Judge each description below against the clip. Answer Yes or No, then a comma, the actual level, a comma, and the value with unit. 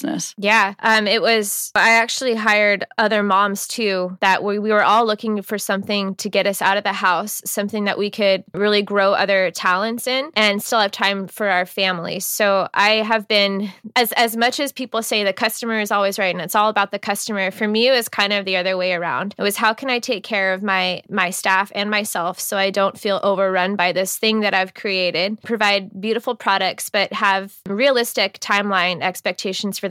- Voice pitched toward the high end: Yes, high, 205 Hz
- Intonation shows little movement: Yes, narrow, 2.1 semitones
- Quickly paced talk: Yes, fast, 210 wpm